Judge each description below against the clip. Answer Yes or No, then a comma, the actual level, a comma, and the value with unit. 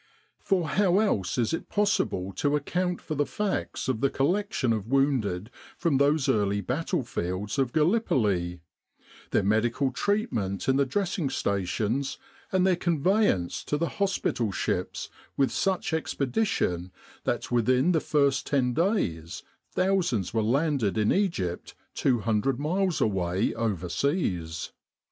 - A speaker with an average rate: No, slow, 130 wpm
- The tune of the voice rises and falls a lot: Yes, wide, 8.9 semitones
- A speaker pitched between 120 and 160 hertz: Yes, low, 135 Hz